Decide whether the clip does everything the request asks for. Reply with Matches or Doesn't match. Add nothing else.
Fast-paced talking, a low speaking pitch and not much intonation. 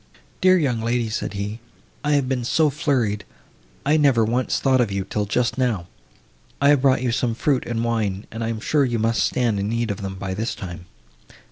Doesn't match